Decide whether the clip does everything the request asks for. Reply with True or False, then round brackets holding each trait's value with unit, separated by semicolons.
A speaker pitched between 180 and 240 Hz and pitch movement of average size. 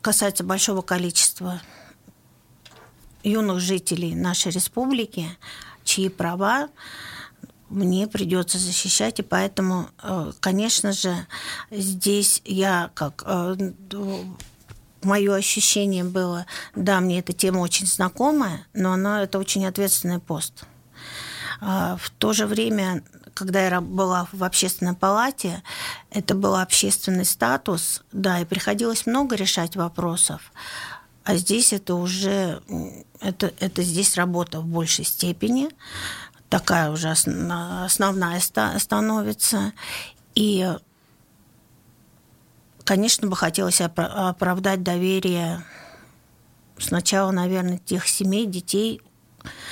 False (190 Hz; 2.2 semitones)